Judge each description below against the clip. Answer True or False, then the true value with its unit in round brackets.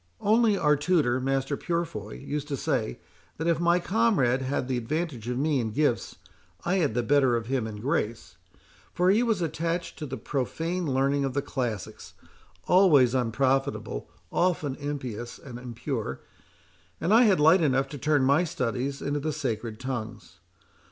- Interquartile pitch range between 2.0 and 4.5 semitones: False (5.1 semitones)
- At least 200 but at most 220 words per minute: False (165 wpm)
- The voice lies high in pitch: False (140 Hz)